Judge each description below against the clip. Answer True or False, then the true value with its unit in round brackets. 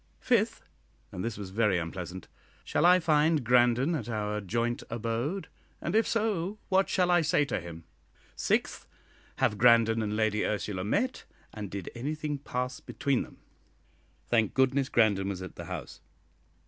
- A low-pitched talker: True (120 Hz)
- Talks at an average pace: True (155 wpm)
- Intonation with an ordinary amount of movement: False (6.8 semitones)